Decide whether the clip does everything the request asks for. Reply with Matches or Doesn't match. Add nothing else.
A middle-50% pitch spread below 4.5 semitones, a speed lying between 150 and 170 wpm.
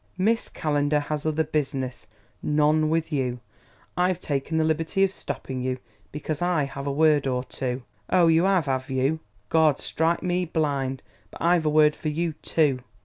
Doesn't match